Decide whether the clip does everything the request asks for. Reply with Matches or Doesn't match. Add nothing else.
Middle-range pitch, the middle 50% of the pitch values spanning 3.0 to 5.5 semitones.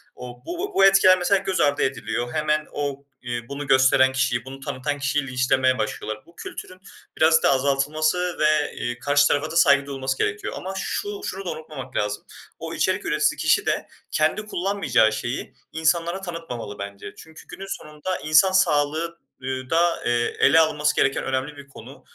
Matches